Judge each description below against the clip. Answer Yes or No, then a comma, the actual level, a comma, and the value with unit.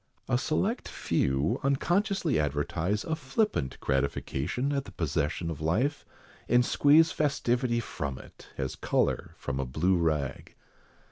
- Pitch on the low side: Yes, low, 100 Hz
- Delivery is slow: Yes, slow, 130 wpm